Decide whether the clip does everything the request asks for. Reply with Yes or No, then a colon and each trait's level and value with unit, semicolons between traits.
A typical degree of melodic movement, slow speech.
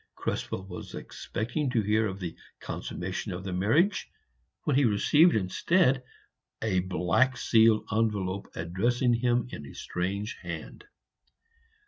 Yes: average, 4.9 semitones; slow, 120 wpm